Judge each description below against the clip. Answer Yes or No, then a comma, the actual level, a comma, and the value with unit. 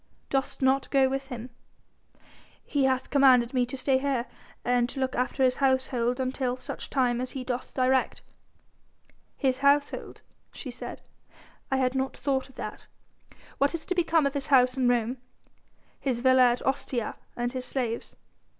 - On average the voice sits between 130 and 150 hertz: No, very high, 260 Hz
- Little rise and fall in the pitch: Yes, narrow, 1.4 semitones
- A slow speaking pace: No, average, 165 wpm